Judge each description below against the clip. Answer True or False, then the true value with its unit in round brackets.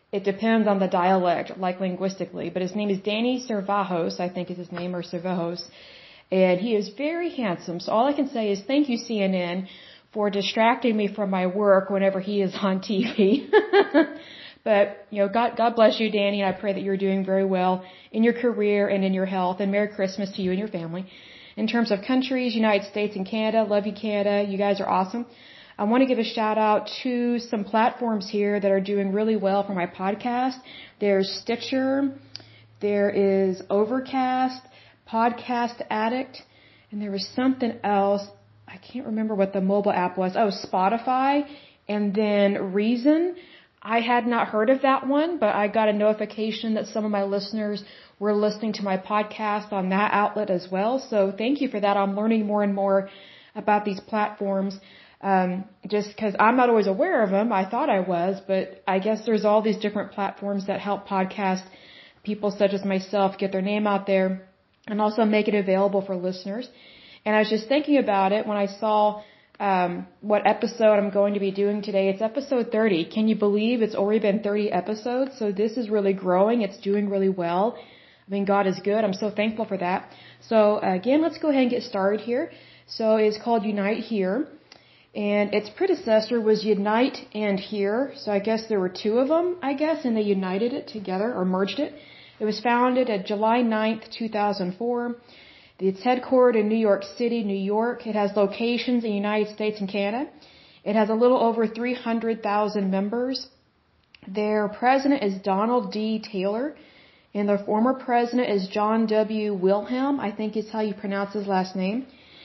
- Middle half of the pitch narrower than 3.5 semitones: True (2.8 semitones)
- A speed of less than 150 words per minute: False (190 wpm)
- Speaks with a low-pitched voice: False (210 Hz)